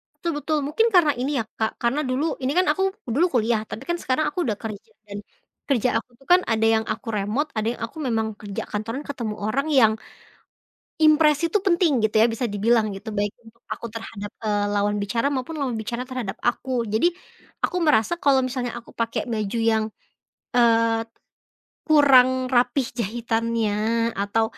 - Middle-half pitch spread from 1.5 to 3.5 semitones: No, average, 4.0 semitones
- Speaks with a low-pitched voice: No, high, 235 Hz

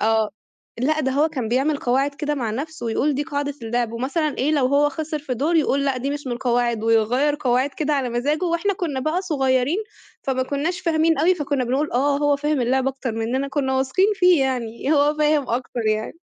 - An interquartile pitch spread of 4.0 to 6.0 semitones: No, average, 3.3 semitones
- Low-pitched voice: No, very high, 275 Hz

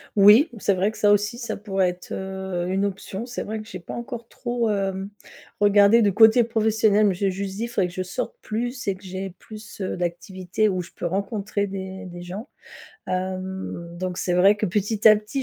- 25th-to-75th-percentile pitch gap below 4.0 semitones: Yes, narrow, 2.5 semitones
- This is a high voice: Yes, high, 200 Hz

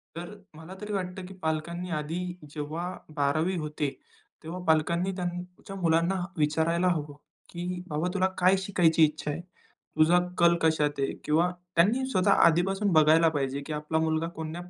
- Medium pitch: Yes, medium, 165 Hz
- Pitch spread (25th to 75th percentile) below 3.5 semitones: Yes, narrow, 2.6 semitones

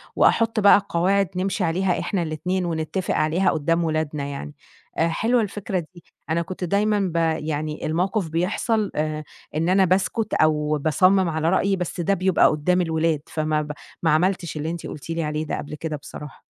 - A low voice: No, medium, 170 Hz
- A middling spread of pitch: Yes, average, 3.5 semitones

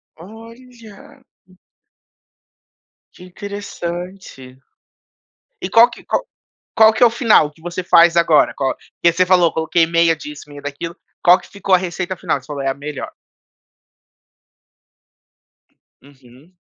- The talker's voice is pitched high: No, medium, 170 Hz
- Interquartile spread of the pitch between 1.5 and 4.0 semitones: No, average, 4.8 semitones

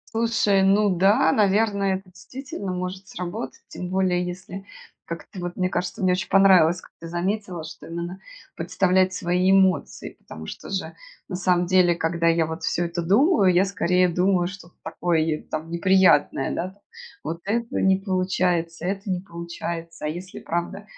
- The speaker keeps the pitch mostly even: Yes, narrow, 2.1 semitones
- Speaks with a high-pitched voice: No, medium, 180 Hz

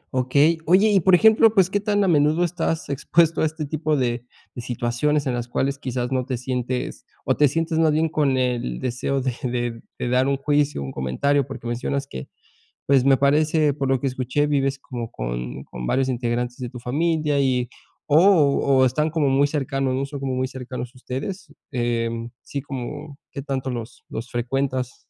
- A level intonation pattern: No, average, 3.3 semitones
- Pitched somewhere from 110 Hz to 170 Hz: Yes, low, 135 Hz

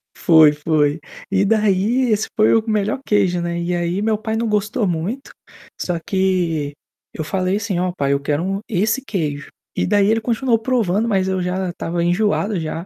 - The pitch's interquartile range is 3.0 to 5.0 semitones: Yes, average, 3.9 semitones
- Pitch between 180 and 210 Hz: Yes, high, 190 Hz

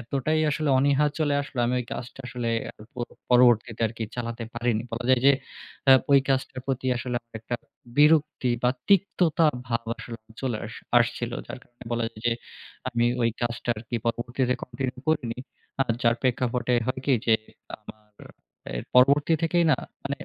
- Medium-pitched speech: No, low, 125 Hz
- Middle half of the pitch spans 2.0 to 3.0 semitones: Yes, narrow, 2.6 semitones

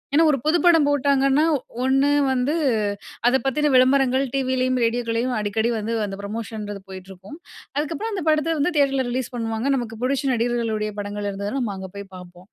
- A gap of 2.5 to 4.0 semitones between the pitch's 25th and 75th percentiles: No, average, 4.6 semitones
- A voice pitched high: Yes, very high, 250 Hz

